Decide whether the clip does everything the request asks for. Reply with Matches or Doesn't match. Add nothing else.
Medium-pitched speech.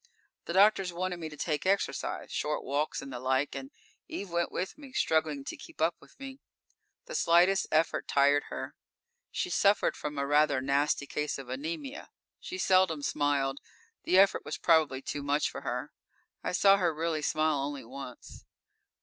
Matches